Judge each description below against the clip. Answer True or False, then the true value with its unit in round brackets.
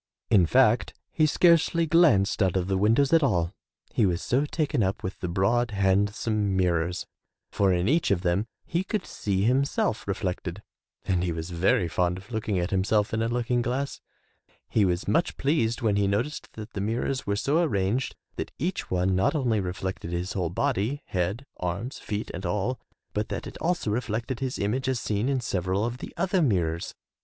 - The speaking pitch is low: True (105 Hz)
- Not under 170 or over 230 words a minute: True (185 wpm)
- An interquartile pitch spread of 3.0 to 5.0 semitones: False (5.5 semitones)